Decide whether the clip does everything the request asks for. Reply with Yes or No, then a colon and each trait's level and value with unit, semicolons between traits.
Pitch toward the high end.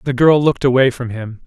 No: low, 130 Hz